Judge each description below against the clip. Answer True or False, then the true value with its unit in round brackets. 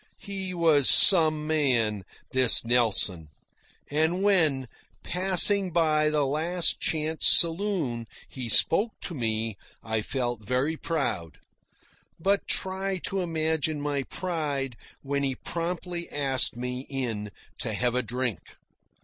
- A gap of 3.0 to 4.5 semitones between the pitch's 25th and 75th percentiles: False (5.4 semitones)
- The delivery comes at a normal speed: False (120 wpm)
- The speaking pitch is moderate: True (150 Hz)